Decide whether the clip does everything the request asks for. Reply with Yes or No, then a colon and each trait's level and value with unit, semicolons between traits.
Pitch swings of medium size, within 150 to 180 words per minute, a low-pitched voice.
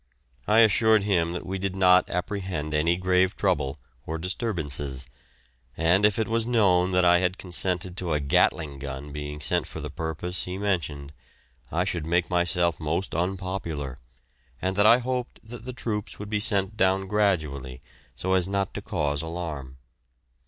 Yes: average, 4.0 semitones; average, 165 wpm; very low, 90 Hz